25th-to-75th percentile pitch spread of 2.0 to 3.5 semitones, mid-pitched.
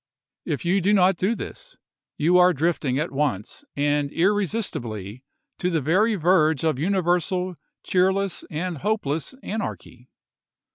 No: average, 4.7 semitones; medium, 175 Hz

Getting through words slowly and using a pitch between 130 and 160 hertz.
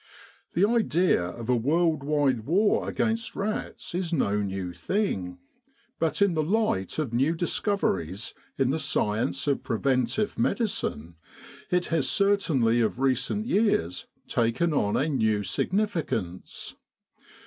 Yes: slow, 130 wpm; medium, 140 Hz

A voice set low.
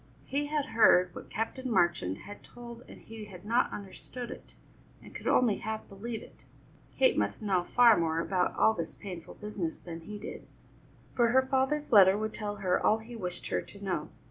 No: high, 210 Hz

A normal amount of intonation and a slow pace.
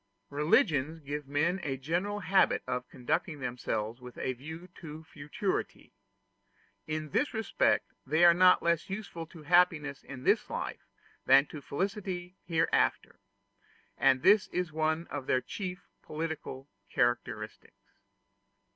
Yes: average, 4.4 semitones; slow, 130 wpm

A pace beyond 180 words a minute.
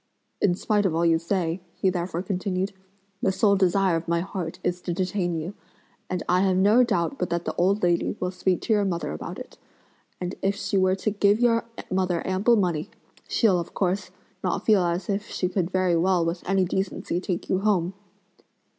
Yes: average, 200 wpm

